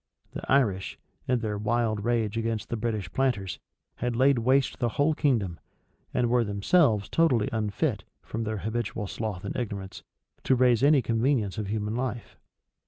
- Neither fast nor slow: Yes, average, 160 wpm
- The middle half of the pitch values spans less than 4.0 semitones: Yes, average, 3.1 semitones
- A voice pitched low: Yes, low, 115 Hz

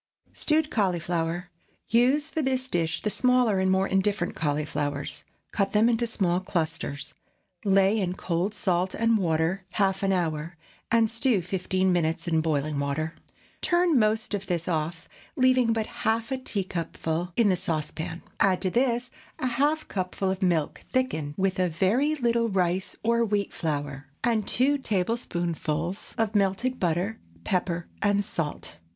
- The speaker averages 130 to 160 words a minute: Yes, average, 150 wpm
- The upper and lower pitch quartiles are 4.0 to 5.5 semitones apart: Yes, average, 5.2 semitones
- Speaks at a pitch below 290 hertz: Yes, high, 190 Hz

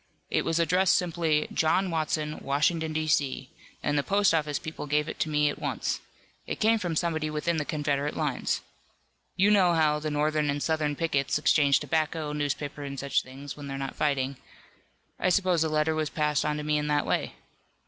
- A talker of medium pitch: Yes, medium, 150 Hz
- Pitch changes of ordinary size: No, narrow, 1.8 semitones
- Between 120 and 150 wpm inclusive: No, average, 195 wpm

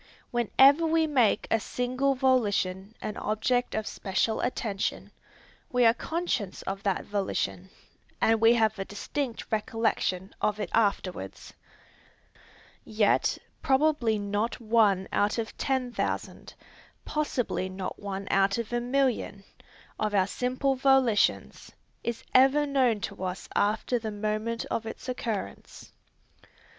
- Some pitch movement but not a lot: Yes, average, 3.8 semitones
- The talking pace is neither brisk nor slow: No, slow, 125 wpm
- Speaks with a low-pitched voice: No, high, 225 Hz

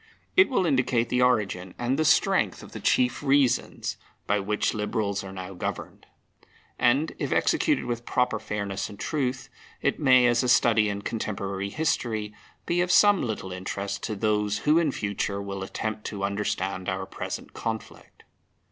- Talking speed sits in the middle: Yes, average, 165 wpm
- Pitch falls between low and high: No, low, 110 Hz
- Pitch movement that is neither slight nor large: Yes, average, 4.2 semitones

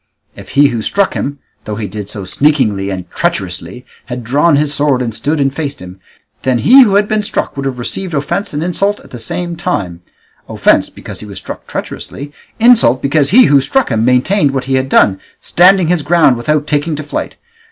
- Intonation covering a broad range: Yes, wide, 6.2 semitones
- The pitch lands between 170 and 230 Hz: No, medium, 140 Hz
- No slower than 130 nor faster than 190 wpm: No, fast, 205 wpm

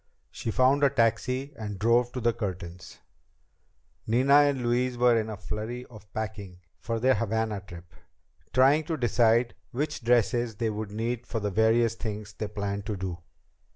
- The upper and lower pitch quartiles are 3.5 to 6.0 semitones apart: No, average, 2.8 semitones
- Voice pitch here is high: No, low, 115 Hz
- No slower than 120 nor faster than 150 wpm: No, average, 165 wpm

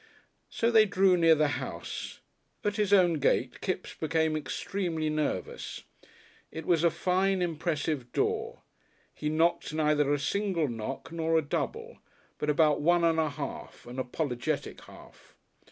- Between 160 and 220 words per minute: No, average, 145 wpm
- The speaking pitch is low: No, medium, 160 Hz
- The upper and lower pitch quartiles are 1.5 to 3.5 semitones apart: Yes, average, 3.2 semitones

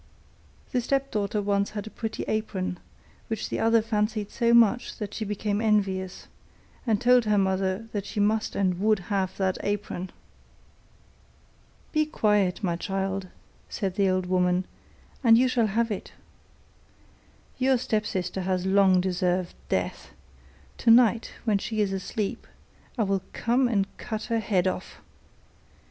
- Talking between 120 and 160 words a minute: Yes, average, 140 wpm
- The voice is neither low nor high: No, high, 205 Hz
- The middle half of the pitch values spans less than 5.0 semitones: Yes, average, 2.9 semitones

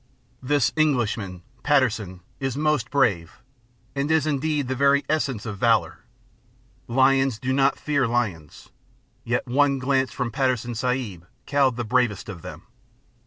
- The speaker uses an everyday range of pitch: Yes, average, 3.9 semitones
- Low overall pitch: Yes, low, 130 Hz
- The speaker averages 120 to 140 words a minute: Yes, slow, 135 wpm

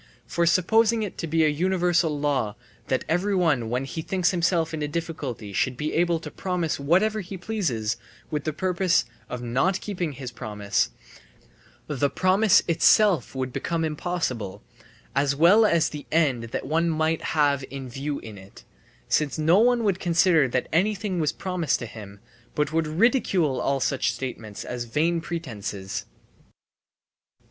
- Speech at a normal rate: Yes, average, 155 wpm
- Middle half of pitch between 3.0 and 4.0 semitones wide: No, average, 5.1 semitones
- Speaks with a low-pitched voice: No, medium, 160 Hz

